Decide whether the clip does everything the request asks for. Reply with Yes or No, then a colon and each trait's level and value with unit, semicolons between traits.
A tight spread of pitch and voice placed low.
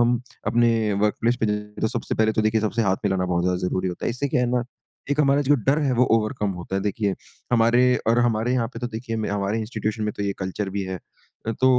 No: average, 3.0 semitones; low, 110 Hz